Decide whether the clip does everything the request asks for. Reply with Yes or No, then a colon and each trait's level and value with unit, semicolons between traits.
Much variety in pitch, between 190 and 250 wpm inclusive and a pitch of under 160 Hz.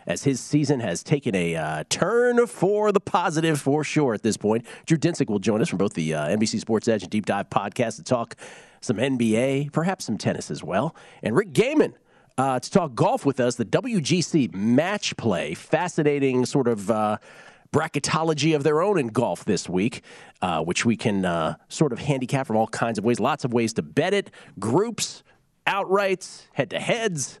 Yes: wide, 6.1 semitones; average, 195 wpm; medium, 140 Hz